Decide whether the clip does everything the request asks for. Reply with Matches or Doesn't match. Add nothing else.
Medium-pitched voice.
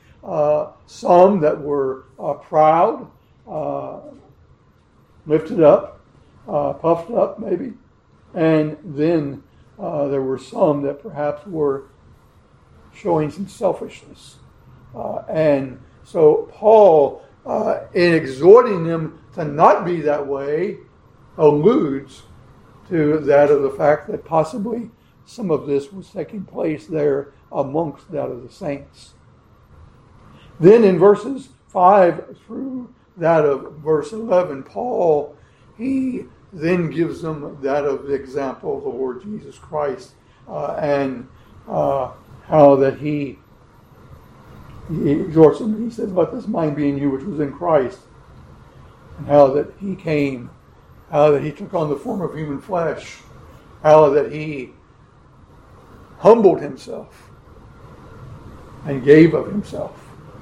Matches